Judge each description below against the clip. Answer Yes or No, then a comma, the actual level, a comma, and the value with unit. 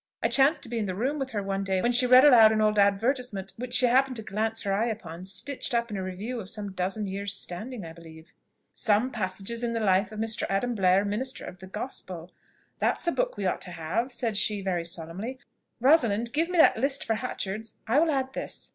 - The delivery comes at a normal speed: No, fast, 235 wpm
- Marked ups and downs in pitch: No, average, 4.5 semitones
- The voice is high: Yes, high, 215 Hz